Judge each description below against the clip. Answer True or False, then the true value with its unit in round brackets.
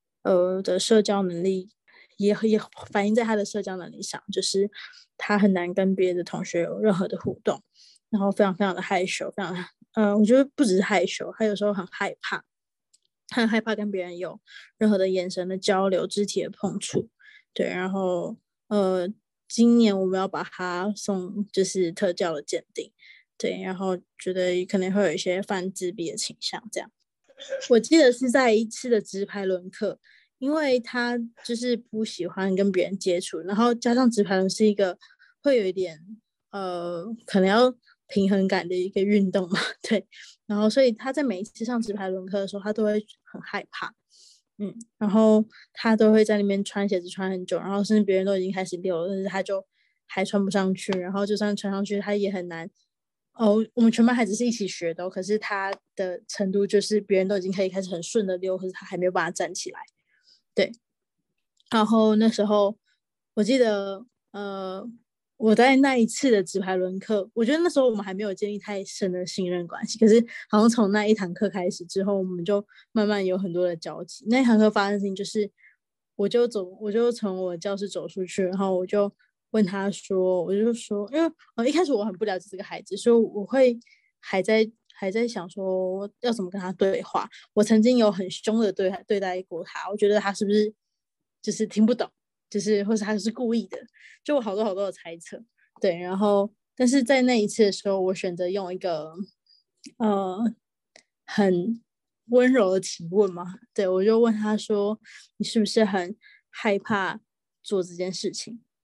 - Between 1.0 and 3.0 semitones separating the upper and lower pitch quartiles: True (2.7 semitones)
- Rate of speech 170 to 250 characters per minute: False (280 characters per minute)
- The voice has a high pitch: True (205 Hz)